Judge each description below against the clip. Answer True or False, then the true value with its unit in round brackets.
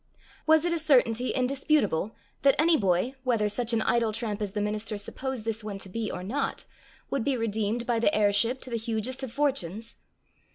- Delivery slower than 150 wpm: False (195 wpm)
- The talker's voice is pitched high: True (230 Hz)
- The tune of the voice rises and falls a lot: False (3.8 semitones)